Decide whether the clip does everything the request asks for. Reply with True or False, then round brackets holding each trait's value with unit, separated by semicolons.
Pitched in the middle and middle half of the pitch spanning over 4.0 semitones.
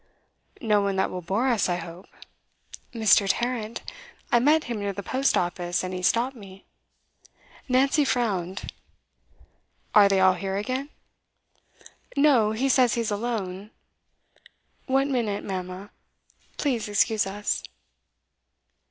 False (210 Hz; 4.4 semitones)